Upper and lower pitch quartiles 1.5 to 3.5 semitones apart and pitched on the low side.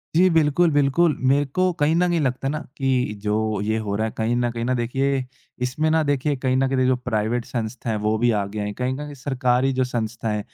No: average, 3.9 semitones; low, 130 Hz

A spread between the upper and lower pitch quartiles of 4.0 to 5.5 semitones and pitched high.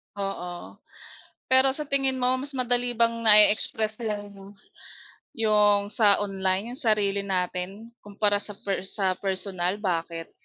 No: average, 3.0 semitones; high, 205 Hz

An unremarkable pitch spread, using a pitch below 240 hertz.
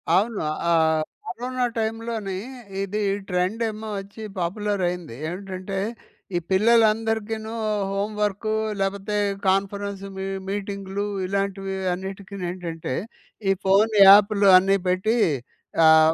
No: narrow, 2.2 semitones; high, 200 Hz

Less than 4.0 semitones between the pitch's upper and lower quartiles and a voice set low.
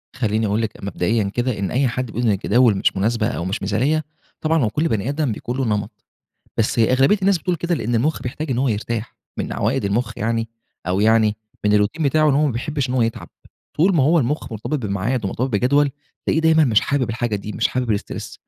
No: average, 4.9 semitones; low, 120 Hz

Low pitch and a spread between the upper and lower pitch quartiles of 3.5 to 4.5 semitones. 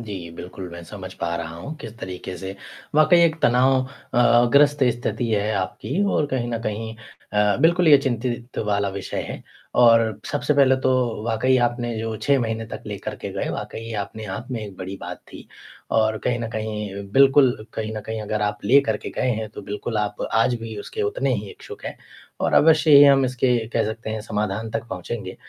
Yes: low, 115 Hz; average, 3.8 semitones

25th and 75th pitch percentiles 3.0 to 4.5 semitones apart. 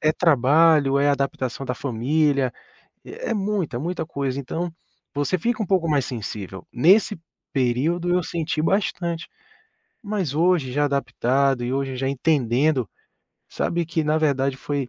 Yes: average, 4.2 semitones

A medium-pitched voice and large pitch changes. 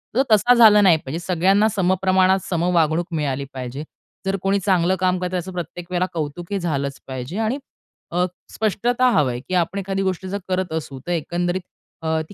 No: medium, 180 Hz; average, 3.2 semitones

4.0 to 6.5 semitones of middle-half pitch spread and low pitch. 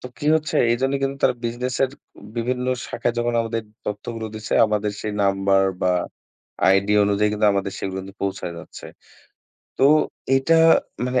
Yes: average, 4.3 semitones; low, 115 Hz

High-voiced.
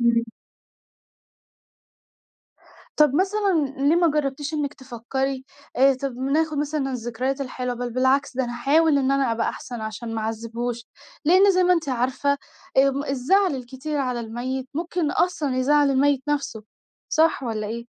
Yes: very high, 270 Hz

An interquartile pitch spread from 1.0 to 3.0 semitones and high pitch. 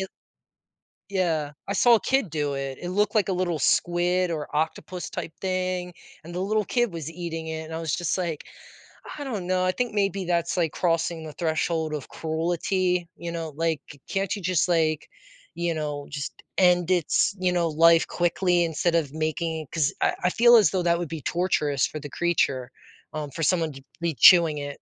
No: narrow, 2.6 semitones; medium, 170 Hz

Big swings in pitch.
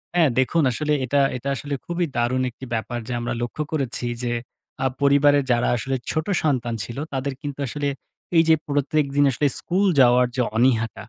No: average, 3.3 semitones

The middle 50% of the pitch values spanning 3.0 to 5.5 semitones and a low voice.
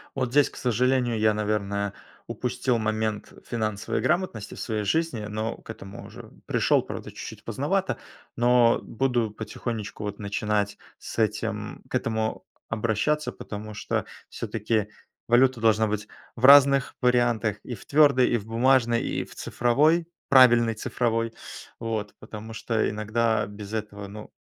No: narrow, 2.5 semitones; low, 115 Hz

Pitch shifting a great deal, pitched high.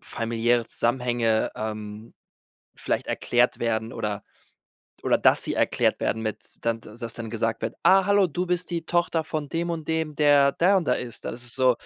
No: wide, 6.1 semitones; low, 120 Hz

